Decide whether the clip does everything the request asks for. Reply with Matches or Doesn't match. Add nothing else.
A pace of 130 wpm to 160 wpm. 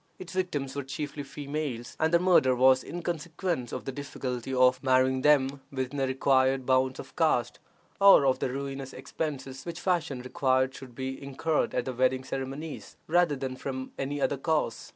Doesn't match